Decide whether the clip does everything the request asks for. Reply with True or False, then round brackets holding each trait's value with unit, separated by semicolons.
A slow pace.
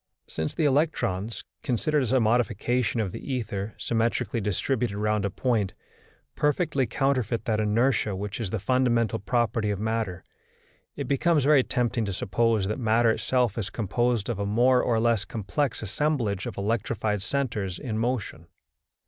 False (155 wpm)